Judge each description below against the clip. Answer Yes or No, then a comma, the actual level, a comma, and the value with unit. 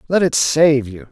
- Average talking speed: No, fast, 215 wpm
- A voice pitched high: No, medium, 140 Hz